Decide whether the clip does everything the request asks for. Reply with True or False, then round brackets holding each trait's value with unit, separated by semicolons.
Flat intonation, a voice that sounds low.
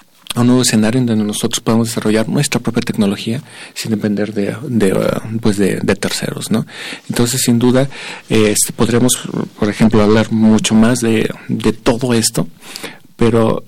True (2.0 semitones; 115 Hz)